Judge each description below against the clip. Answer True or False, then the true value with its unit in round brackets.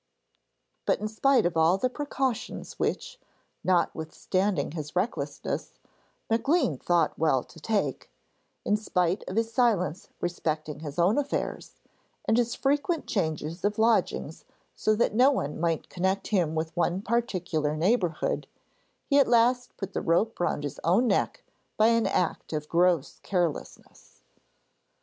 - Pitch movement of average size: False (6.0 semitones)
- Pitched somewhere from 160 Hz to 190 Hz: True (185 Hz)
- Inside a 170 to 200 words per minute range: False (140 wpm)